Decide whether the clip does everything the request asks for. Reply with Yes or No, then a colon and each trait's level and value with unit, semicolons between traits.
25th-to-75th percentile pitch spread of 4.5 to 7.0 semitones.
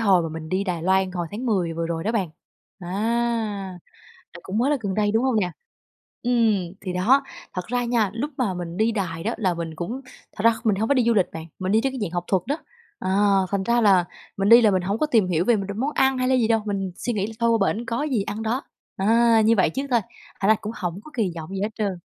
No: average, 4.1 semitones